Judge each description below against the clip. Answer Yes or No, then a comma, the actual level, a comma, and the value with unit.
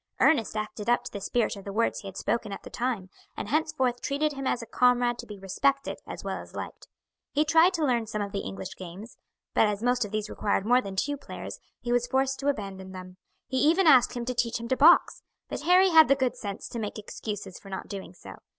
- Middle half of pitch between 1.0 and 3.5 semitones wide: No, average, 4.8 semitones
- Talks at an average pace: No, fast, 245 wpm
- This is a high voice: Yes, high, 235 Hz